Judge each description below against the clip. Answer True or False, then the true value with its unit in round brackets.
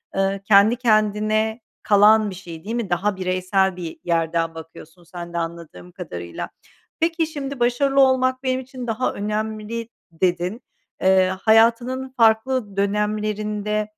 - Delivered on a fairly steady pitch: False (4.3 semitones)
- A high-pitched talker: True (210 Hz)